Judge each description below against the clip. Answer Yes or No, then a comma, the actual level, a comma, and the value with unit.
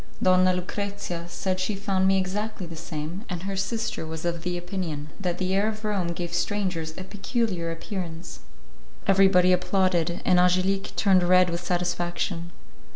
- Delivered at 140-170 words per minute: Yes, average, 155 wpm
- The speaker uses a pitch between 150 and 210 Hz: Yes, medium, 185 Hz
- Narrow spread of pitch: Yes, narrow, 2.1 semitones